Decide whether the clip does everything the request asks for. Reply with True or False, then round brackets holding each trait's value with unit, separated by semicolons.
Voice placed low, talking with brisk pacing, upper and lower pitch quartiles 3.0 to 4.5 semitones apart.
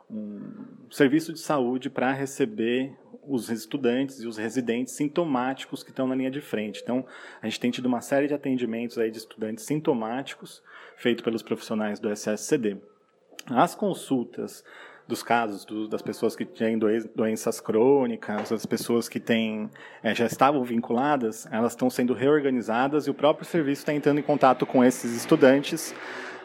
False (125 Hz; 160 wpm; 4.0 semitones)